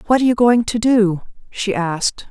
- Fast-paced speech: Yes, fast, 210 wpm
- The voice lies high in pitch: Yes, high, 220 Hz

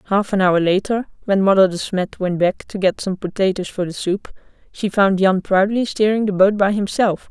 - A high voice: Yes, high, 195 Hz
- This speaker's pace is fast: Yes, fast, 215 wpm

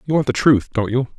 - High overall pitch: No, low, 125 Hz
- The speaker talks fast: Yes, fast, 305 wpm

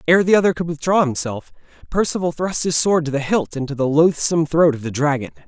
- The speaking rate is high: Yes, fast, 220 wpm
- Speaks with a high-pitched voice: No, medium, 155 Hz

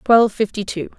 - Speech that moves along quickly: No, average, 185 wpm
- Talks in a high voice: Yes, high, 210 Hz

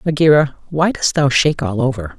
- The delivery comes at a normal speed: Yes, average, 190 wpm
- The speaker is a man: Yes, male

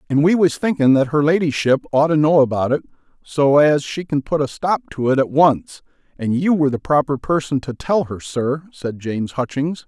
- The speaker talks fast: Yes, fast, 220 wpm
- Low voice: No, medium, 145 Hz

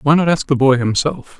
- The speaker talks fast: Yes, fast, 260 wpm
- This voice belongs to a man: Yes, male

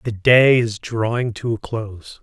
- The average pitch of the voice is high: No, low, 110 Hz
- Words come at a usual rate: Yes, average, 190 wpm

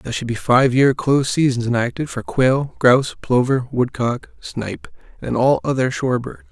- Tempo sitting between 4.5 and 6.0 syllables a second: Yes, 5.1 syllables/s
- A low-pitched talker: Yes, low, 130 Hz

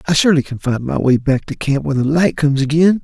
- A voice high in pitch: No, medium, 140 Hz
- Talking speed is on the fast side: Yes, fast, 275 wpm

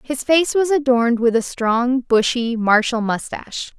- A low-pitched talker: No, high, 245 Hz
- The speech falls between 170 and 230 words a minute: No, average, 160 wpm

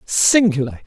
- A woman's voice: Yes, female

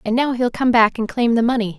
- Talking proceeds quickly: Yes, fast, 305 wpm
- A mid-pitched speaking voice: No, high, 235 Hz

